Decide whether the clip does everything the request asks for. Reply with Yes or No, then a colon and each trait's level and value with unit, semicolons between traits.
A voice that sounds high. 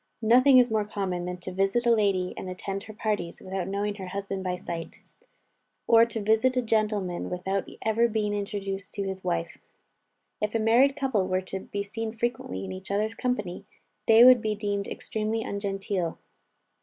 Yes: high, 205 Hz